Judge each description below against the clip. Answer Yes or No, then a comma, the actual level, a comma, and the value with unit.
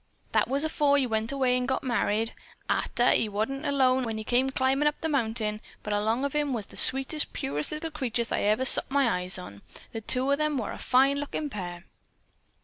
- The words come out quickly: Yes, fast, 220 wpm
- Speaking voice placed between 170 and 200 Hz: No, very high, 255 Hz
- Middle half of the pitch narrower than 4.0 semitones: No, average, 4.3 semitones